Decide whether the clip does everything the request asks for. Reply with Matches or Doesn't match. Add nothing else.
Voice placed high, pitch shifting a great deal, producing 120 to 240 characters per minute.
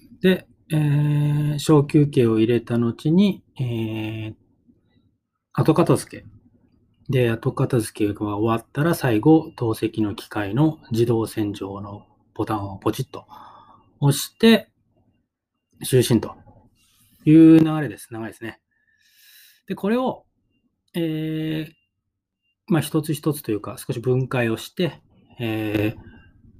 Doesn't match